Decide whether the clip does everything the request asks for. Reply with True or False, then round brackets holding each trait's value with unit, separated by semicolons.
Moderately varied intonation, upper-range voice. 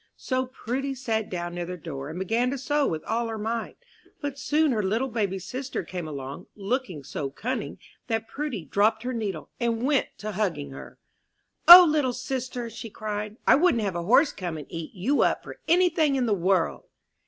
False (6.2 semitones; 225 Hz)